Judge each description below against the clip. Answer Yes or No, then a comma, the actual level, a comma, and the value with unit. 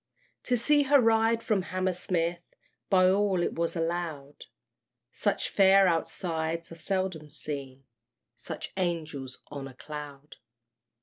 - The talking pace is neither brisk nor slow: No, slow, 120 wpm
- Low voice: No, medium, 175 Hz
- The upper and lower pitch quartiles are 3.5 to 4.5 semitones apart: Yes, average, 4.1 semitones